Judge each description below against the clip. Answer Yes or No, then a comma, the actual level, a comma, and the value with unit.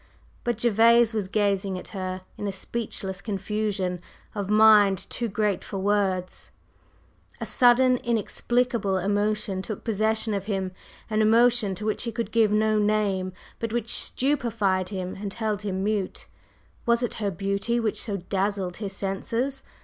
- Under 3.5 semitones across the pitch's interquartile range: Yes, average, 2.7 semitones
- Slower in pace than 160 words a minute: Yes, average, 150 wpm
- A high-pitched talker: Yes, high, 210 Hz